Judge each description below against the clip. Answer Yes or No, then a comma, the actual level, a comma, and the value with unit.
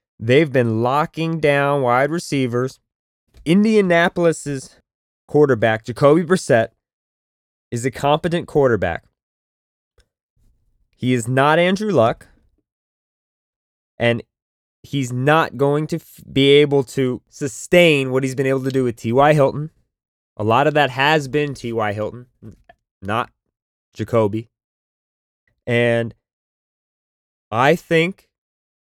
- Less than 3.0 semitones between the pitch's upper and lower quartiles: No, average, 4.5 semitones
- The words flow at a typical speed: No, slow, 105 wpm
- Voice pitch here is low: Yes, low, 130 Hz